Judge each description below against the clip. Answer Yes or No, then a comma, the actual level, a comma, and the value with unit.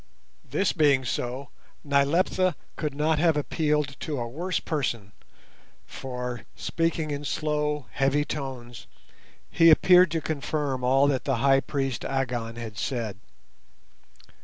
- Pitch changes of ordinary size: Yes, average, 3.2 semitones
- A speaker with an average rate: No, slow, 125 wpm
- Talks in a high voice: No, medium, 140 Hz